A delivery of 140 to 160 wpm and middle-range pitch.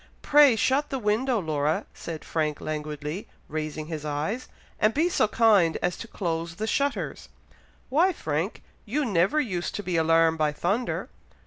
Yes: average, 155 wpm; medium, 180 Hz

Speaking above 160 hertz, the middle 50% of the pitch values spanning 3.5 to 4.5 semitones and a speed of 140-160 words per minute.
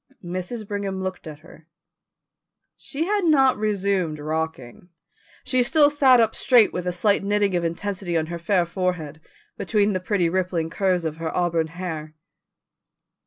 Yes: medium, 185 Hz; average, 3.9 semitones; average, 155 wpm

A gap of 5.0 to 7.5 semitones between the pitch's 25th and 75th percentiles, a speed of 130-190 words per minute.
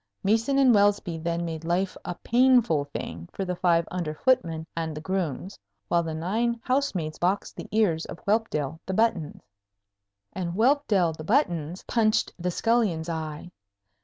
Yes: wide, 5.4 semitones; average, 160 wpm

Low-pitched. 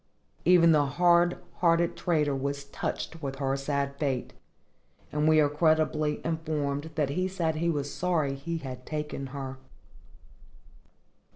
No: medium, 150 Hz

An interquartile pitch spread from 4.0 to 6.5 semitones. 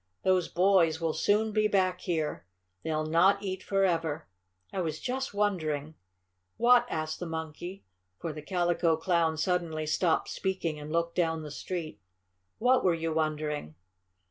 No: average, 3.2 semitones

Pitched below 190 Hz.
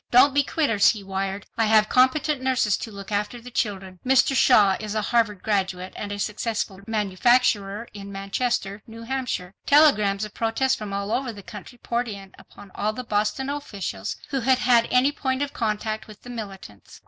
No: high, 215 Hz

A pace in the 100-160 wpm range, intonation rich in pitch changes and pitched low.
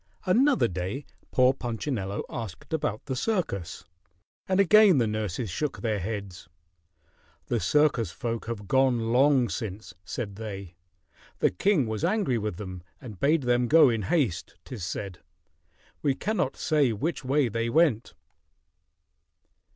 Yes: slow, 135 wpm; wide, 6.0 semitones; low, 120 Hz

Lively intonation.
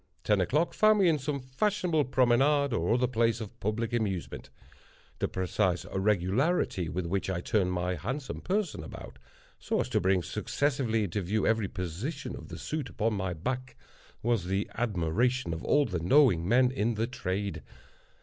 Yes: wide, 6.0 semitones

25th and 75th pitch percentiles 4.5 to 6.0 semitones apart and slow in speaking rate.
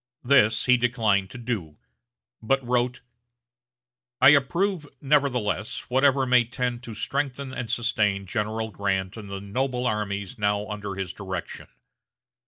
No: average, 3.9 semitones; slow, 130 wpm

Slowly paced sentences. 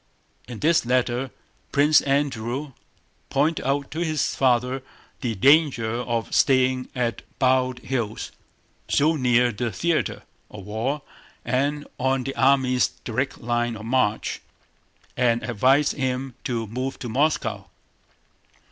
Yes: slow, 120 wpm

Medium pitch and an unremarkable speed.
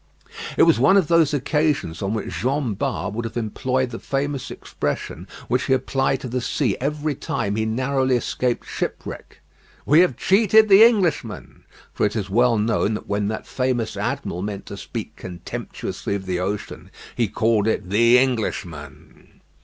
No: low, 120 Hz; average, 170 wpm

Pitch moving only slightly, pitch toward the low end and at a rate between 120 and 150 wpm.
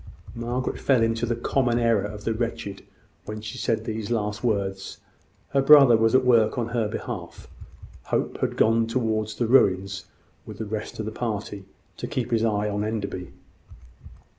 No: narrow, 2.1 semitones; low, 110 Hz; average, 170 wpm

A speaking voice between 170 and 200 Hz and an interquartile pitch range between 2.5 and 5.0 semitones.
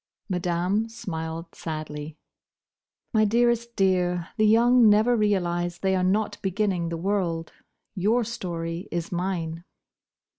Yes: medium, 185 Hz; average, 4.1 semitones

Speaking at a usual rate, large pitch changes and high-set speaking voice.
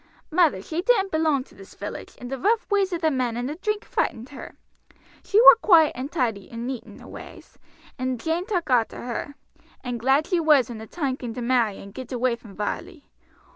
No: fast, 215 wpm; wide, 5.8 semitones; very high, 265 Hz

